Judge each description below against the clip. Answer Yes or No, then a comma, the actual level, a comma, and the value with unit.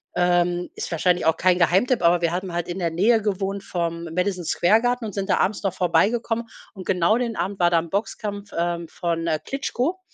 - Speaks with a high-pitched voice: No, medium, 180 Hz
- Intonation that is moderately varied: Yes, average, 3.1 semitones